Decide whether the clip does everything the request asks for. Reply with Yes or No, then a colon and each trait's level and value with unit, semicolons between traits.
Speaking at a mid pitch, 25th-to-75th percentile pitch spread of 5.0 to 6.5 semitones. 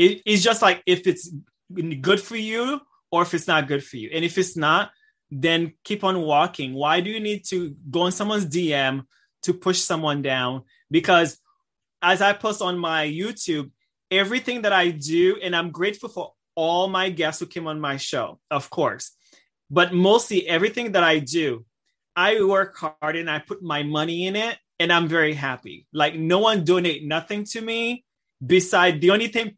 No: medium, 180 Hz; average, 4.4 semitones